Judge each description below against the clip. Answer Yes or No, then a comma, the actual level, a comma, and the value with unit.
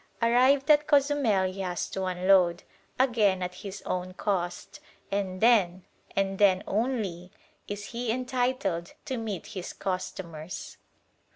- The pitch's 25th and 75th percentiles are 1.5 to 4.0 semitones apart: No, average, 4.8 semitones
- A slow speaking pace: Yes, slow, 125 wpm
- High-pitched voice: Yes, high, 195 Hz